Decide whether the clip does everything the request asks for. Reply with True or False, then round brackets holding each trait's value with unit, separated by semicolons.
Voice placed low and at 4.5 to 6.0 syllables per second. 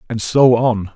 False (115 Hz; 3.9 syllables/s)